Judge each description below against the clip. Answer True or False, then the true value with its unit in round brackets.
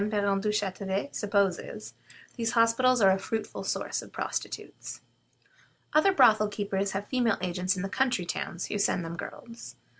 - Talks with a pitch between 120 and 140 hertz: False (205 Hz)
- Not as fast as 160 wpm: True (150 wpm)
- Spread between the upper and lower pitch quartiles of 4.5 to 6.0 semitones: False (3.1 semitones)